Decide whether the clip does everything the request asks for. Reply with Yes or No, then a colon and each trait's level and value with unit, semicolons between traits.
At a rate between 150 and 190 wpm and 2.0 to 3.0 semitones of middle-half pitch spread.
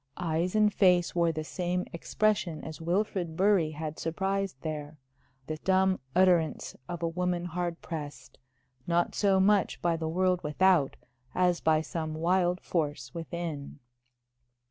No: average, 140 wpm; narrow, 2.6 semitones